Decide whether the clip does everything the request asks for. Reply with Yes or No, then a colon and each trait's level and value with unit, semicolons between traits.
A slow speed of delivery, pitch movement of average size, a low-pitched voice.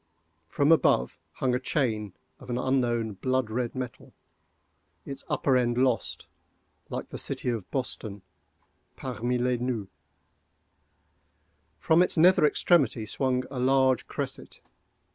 Yes: slow, 120 wpm; average, 3.1 semitones; low, 125 Hz